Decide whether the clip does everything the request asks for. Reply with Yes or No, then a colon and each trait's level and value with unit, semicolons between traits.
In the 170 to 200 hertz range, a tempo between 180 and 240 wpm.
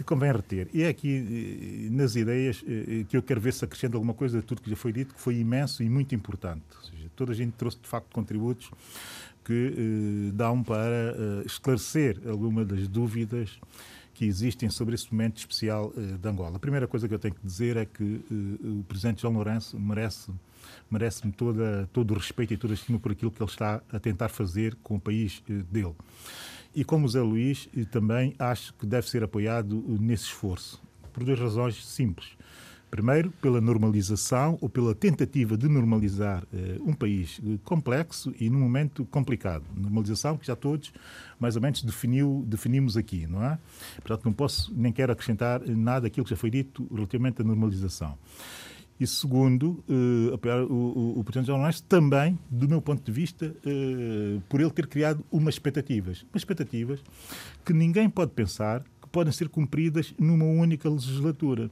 No: low, 120 Hz; fast, 185 wpm